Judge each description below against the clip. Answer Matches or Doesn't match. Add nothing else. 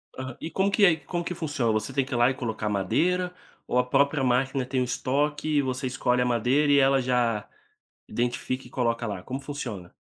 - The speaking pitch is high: Doesn't match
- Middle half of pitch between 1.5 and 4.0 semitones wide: Matches